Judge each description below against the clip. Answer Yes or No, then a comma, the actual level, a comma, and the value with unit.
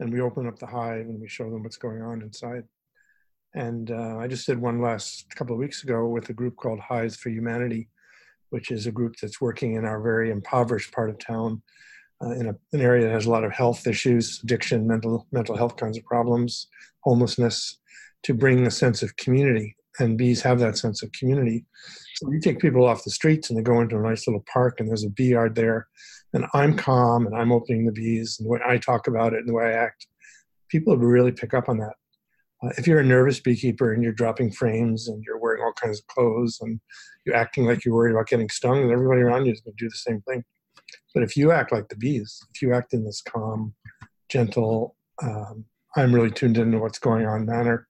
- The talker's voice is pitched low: Yes, low, 120 Hz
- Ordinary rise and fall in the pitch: No, narrow, 1.5 semitones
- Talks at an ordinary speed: No, fast, 230 wpm